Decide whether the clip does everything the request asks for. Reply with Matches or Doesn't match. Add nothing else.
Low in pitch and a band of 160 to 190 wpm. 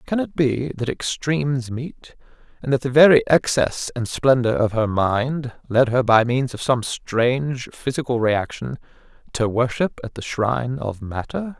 Matches